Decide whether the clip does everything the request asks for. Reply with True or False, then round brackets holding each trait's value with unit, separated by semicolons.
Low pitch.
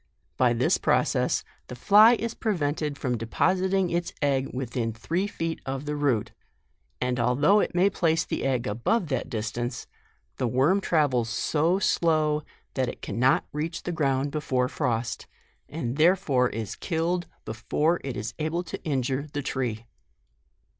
False (145 Hz)